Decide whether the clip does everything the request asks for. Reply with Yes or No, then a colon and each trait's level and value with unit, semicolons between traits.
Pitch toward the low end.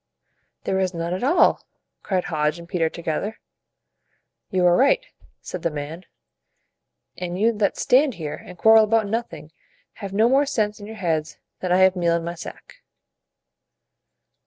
No: medium, 185 Hz